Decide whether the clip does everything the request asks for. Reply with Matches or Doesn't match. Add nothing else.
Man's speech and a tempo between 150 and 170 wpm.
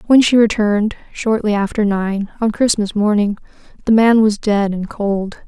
Doesn't match